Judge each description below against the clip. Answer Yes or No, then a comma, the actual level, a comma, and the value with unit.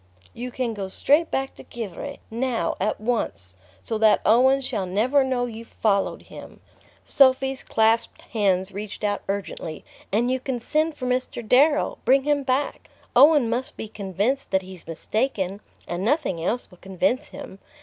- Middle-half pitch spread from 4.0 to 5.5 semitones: Yes, average, 4.8 semitones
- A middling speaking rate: Yes, average, 160 wpm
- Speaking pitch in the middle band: No, high, 230 Hz